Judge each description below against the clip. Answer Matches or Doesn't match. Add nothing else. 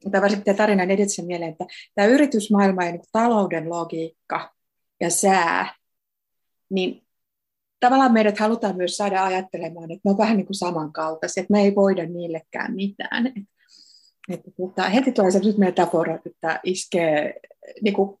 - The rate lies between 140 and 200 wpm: Matches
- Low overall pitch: Doesn't match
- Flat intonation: Doesn't match